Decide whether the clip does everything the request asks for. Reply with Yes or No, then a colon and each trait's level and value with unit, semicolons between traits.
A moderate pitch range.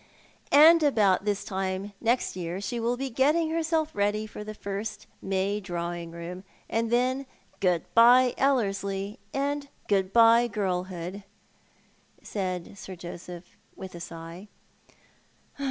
Yes: average, 4.6 semitones